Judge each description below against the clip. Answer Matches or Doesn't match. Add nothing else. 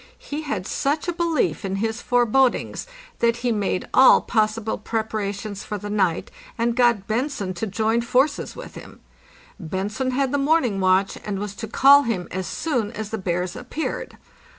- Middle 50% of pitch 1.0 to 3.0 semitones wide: Doesn't match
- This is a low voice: Doesn't match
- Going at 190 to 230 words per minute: Doesn't match